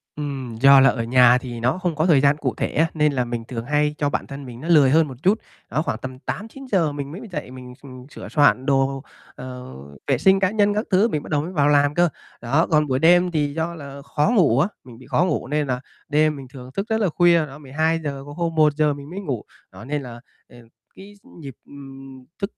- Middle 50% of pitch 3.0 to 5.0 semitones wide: Yes, average, 3.8 semitones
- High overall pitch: No, medium, 145 Hz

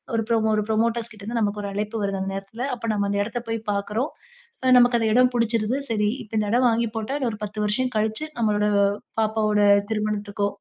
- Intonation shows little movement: Yes, narrow, 2.0 semitones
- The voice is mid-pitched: No, high, 220 Hz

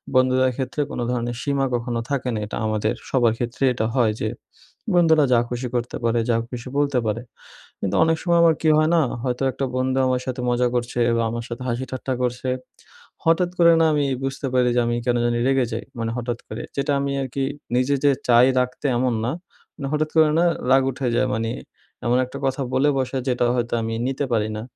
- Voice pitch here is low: Yes, low, 125 Hz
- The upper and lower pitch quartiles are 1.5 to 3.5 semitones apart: Yes, narrow, 2.5 semitones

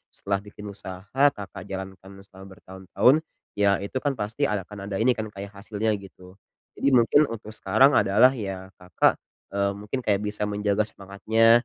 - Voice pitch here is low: Yes, low, 100 Hz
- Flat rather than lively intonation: Yes, narrow, 2.3 semitones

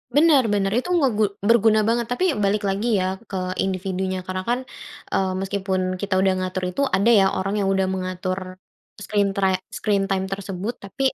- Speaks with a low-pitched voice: No, high, 195 Hz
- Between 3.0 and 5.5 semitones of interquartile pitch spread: No, narrow, 2.5 semitones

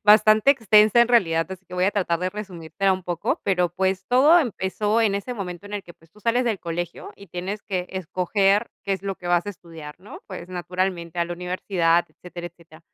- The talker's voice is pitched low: No, medium, 185 Hz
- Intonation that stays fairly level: No, average, 3.0 semitones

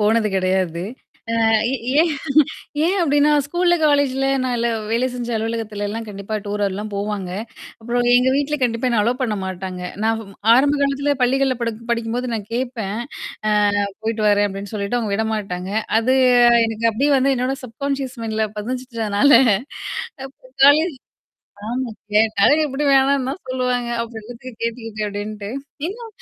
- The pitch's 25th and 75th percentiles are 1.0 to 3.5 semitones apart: No, average, 4.0 semitones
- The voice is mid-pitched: No, high, 230 Hz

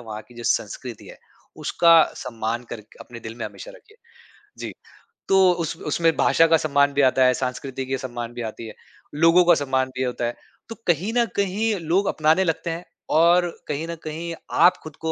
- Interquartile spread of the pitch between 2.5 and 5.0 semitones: No, wide, 5.4 semitones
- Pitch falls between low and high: Yes, medium, 155 Hz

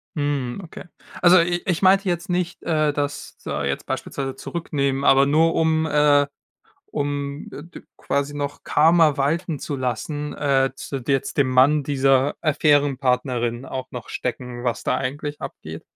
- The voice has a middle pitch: Yes, medium, 145 Hz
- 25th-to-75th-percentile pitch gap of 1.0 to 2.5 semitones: No, average, 2.9 semitones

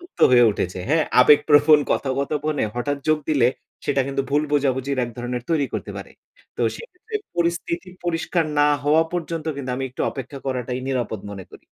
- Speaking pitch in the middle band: Yes, medium, 145 Hz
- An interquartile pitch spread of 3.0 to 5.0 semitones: Yes, average, 3.6 semitones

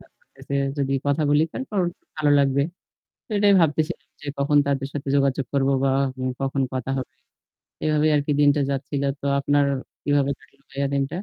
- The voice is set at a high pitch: No, medium, 140 Hz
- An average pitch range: No, narrow, 1.4 semitones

